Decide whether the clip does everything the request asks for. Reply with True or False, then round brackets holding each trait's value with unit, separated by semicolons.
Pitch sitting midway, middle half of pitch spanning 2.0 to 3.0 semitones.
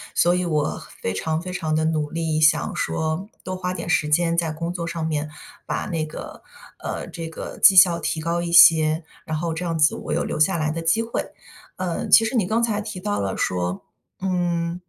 True (170 Hz; 2.5 semitones)